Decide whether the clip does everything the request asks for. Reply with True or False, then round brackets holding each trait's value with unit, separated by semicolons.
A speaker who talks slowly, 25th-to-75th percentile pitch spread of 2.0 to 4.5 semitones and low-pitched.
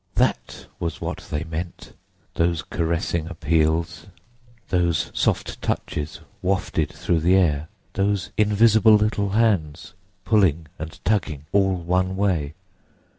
True (115 wpm; 3.7 semitones; 85 Hz)